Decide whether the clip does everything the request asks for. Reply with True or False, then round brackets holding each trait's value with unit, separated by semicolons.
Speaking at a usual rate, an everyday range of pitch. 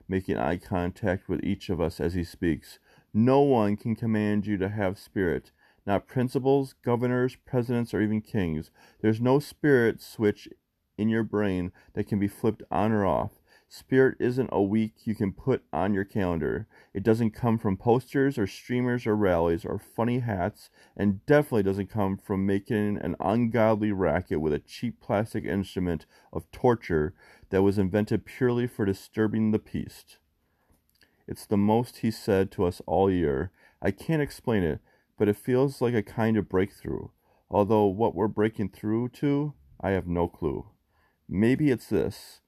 True (170 wpm; 3.6 semitones)